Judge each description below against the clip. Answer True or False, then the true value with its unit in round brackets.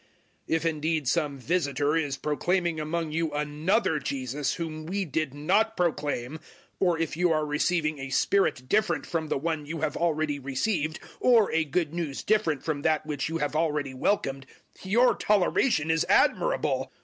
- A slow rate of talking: False (165 wpm)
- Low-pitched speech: False (155 Hz)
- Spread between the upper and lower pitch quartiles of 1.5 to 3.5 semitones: True (2.7 semitones)